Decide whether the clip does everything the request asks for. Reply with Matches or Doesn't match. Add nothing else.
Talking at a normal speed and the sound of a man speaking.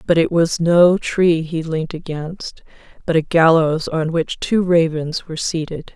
Doesn't match